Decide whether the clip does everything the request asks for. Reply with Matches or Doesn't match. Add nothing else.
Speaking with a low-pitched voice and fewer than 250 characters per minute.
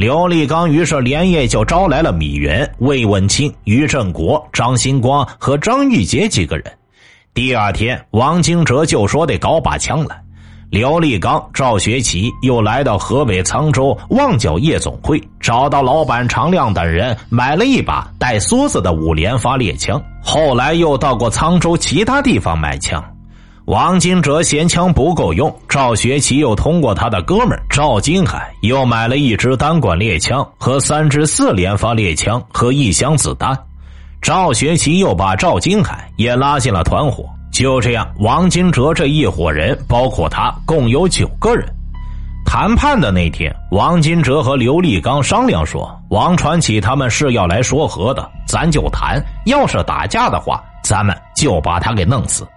Matches